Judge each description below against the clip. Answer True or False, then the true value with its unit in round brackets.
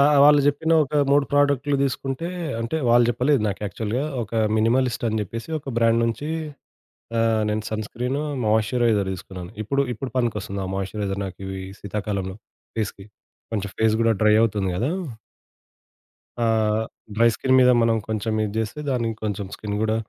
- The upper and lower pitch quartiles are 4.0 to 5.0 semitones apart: False (3.3 semitones)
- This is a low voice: True (115 Hz)